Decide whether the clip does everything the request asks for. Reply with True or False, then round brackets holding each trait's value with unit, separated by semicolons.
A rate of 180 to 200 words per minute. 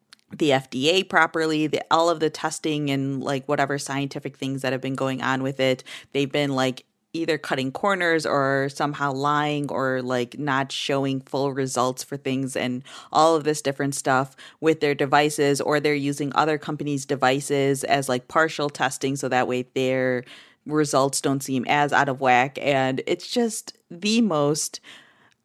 False (170 wpm)